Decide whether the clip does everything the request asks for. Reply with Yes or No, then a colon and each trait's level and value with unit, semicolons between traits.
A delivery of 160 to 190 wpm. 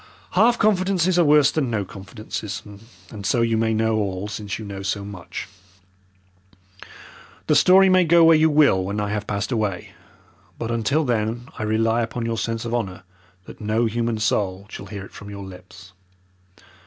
Yes: average, 180 wpm